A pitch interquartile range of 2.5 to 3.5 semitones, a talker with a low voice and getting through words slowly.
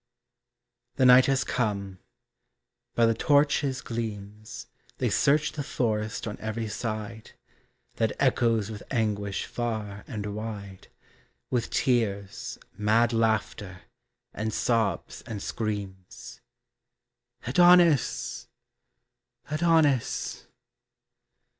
Yes: average, 3.2 semitones; low, 110 Hz; slow, 90 wpm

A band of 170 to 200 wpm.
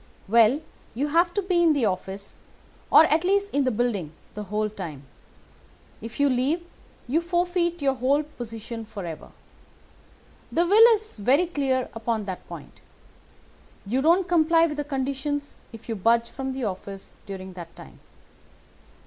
No: average, 155 wpm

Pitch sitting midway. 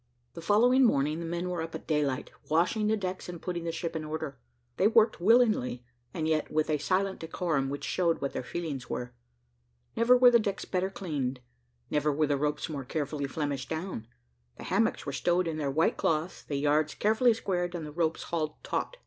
Yes: medium, 165 Hz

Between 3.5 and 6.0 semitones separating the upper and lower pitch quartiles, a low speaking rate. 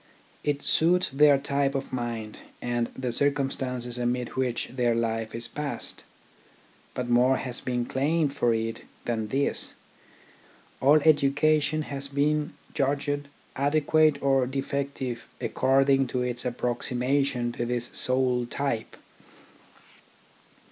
No: average, 2.7 semitones; slow, 115 wpm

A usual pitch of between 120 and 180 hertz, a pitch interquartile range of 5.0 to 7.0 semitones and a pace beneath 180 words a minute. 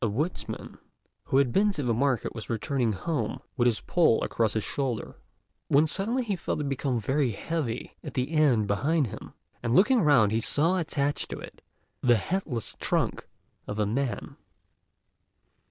Yes: low, 135 Hz; wide, 5.5 semitones; average, 165 wpm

